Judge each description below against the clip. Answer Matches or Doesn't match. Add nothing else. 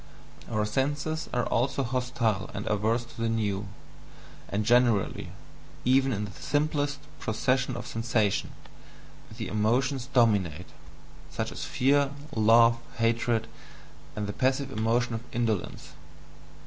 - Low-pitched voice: Matches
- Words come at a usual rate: Doesn't match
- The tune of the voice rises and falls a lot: Doesn't match